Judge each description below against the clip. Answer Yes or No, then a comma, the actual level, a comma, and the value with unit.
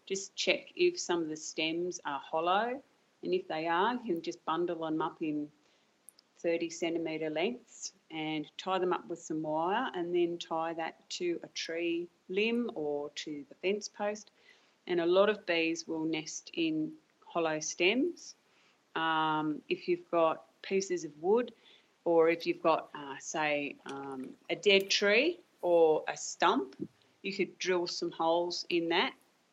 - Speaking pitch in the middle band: Yes, medium, 170 Hz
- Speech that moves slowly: No, average, 165 wpm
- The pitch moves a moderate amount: Yes, average, 3.9 semitones